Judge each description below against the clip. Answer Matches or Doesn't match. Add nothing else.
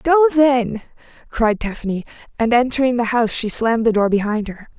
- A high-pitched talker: Matches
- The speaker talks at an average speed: Matches